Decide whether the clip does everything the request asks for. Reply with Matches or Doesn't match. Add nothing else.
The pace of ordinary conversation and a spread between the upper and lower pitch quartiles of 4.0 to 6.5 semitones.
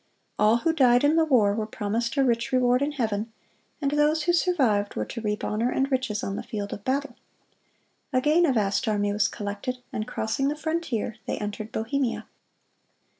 Matches